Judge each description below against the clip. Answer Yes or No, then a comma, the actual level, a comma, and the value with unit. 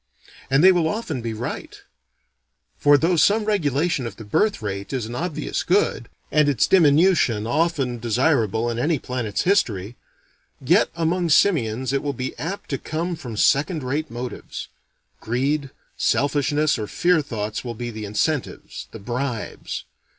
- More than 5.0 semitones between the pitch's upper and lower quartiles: Yes, wide, 5.5 semitones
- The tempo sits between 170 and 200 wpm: No, average, 150 wpm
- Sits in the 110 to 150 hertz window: Yes, low, 135 Hz